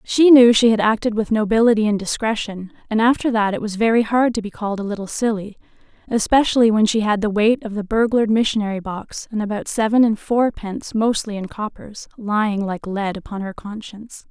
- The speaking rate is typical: Yes, average, 195 wpm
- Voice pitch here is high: Yes, high, 215 Hz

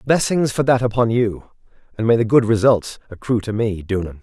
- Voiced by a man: Yes, male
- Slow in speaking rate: No, average, 200 wpm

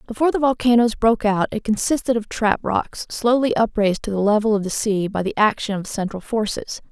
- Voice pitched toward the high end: Yes, high, 220 Hz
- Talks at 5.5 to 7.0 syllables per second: Yes, 5.8 syllables/s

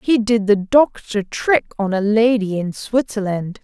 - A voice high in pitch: Yes, high, 215 Hz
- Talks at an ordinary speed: Yes, average, 165 wpm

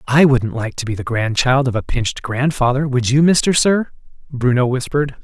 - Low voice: Yes, low, 130 Hz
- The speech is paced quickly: No, average, 195 wpm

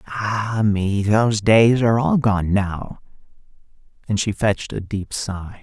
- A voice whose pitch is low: Yes, low, 105 Hz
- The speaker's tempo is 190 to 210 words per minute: No, average, 150 wpm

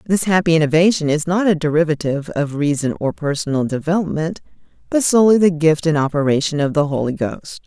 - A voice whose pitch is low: No, medium, 160 Hz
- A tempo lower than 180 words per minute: Yes, average, 170 wpm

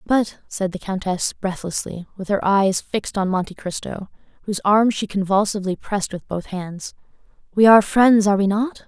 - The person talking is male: No, female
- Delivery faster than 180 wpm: No, average, 175 wpm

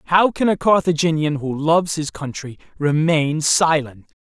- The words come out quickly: No, average, 140 wpm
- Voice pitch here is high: No, medium, 155 Hz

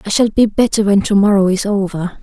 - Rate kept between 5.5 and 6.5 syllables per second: Yes, 5.7 syllables/s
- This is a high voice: Yes, high, 200 Hz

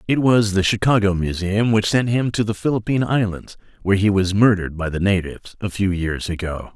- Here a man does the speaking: Yes, male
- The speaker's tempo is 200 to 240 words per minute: Yes, fast, 205 wpm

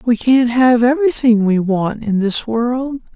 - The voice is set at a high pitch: Yes, high, 240 Hz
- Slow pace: No, average, 170 wpm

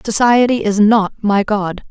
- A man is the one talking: No, female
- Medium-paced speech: Yes, average, 155 wpm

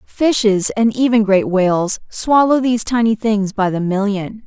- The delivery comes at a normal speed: Yes, average, 160 wpm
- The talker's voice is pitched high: Yes, high, 215 Hz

